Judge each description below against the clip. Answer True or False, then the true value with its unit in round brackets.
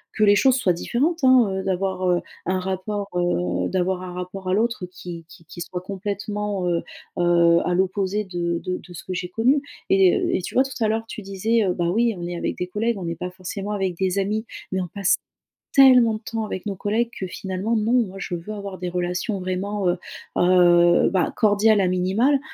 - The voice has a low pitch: False (190 Hz)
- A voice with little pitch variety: False (3.0 semitones)